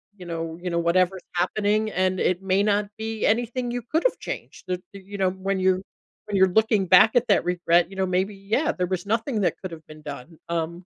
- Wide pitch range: No, average, 3.1 semitones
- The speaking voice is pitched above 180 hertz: Yes, high, 190 Hz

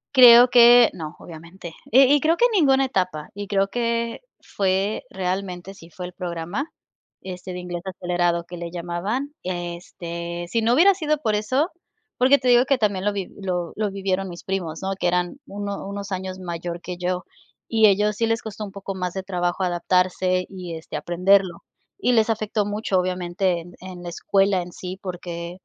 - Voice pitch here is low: No, high, 190 Hz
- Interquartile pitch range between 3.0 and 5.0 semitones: Yes, average, 3.3 semitones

